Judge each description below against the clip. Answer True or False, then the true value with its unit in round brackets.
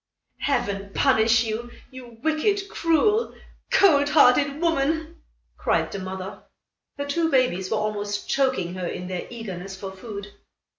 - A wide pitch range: True (6.6 semitones)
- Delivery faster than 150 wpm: False (135 wpm)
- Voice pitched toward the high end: True (240 Hz)